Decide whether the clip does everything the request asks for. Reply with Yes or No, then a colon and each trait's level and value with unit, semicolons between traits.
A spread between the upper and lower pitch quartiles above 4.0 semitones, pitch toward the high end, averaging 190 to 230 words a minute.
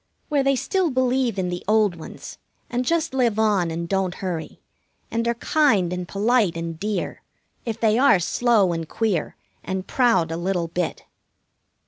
No: wide, 5.6 semitones; high, 205 Hz; average, 165 wpm